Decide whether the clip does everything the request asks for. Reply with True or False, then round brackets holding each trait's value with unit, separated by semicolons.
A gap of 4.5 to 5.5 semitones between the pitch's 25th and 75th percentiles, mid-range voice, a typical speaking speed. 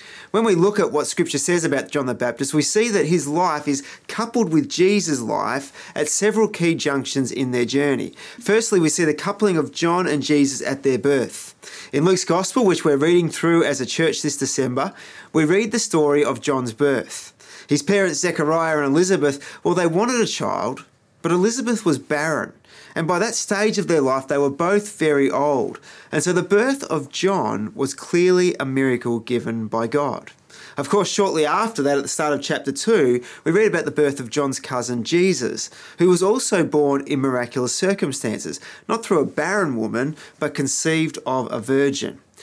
True (5.0 semitones; 150 Hz; 190 wpm)